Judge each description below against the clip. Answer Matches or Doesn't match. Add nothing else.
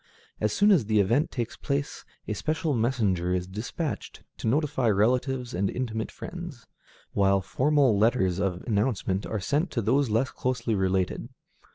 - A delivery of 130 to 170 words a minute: Matches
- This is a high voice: Doesn't match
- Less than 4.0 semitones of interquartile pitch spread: Doesn't match